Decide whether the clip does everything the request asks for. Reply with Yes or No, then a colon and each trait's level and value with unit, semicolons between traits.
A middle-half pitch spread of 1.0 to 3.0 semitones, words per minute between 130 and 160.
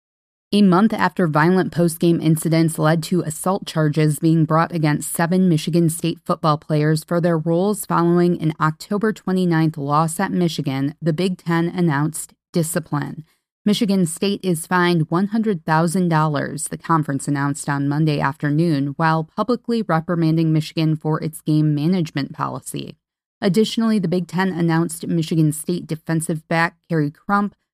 Yes: narrow, 2.6 semitones; average, 140 wpm